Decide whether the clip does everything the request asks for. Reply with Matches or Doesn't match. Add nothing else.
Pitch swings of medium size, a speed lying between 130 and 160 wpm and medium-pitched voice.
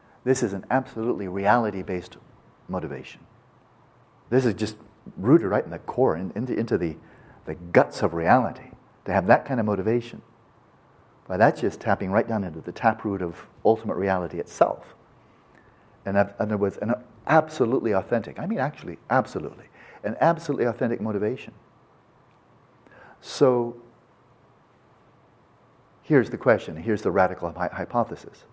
Doesn't match